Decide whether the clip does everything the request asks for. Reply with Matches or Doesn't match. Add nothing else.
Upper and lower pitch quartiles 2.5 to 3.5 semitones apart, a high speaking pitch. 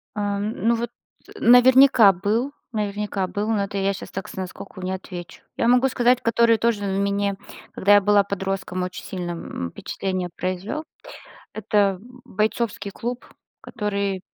Matches